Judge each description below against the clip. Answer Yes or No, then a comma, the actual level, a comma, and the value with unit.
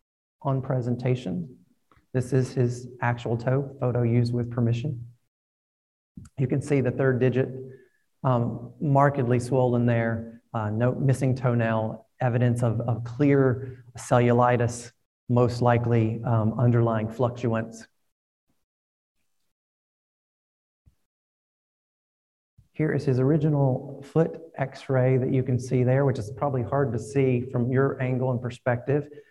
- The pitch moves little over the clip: Yes, narrow, 2.0 semitones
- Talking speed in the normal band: No, slow, 120 wpm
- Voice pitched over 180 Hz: No, low, 125 Hz